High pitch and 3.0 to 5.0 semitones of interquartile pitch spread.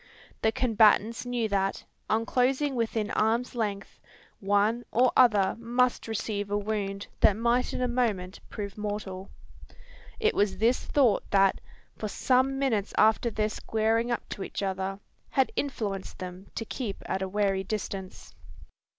Yes: high, 215 Hz; average, 3.3 semitones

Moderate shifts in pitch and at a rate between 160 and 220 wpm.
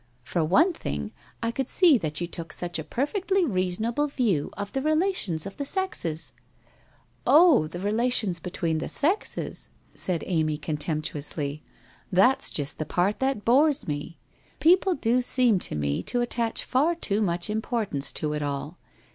No: wide, 9.0 semitones; average, 170 wpm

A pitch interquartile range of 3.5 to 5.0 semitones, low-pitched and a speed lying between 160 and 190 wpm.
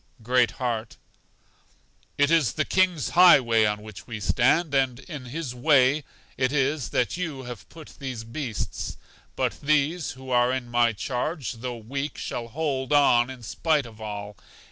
Yes: average, 3.8 semitones; low, 130 Hz; average, 165 wpm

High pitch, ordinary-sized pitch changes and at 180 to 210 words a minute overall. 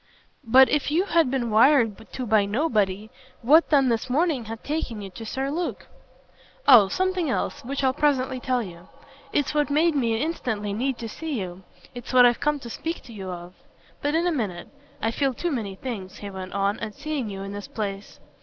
No: high, 245 Hz; wide, 5.9 semitones; fast, 205 wpm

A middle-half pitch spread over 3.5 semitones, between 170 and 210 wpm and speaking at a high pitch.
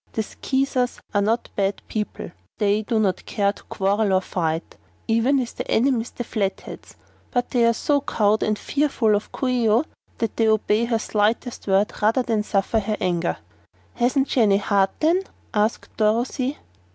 No: average, 3.1 semitones; average, 175 wpm; high, 220 Hz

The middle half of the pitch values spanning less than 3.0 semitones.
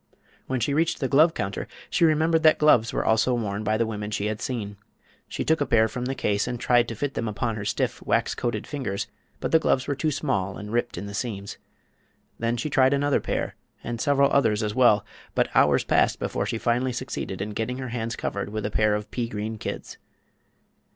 No: average, 4.0 semitones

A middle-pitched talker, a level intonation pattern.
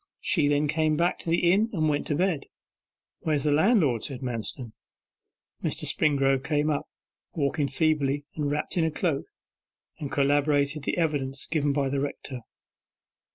Yes: medium, 145 Hz; narrow, 2.1 semitones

